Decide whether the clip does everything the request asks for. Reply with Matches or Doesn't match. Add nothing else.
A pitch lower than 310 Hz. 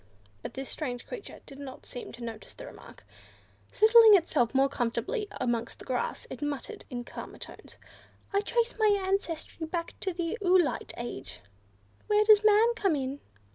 Doesn't match